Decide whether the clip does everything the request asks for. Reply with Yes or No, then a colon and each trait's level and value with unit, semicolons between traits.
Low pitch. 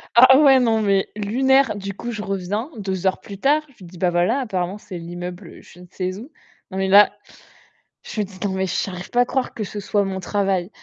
No: high, 200 Hz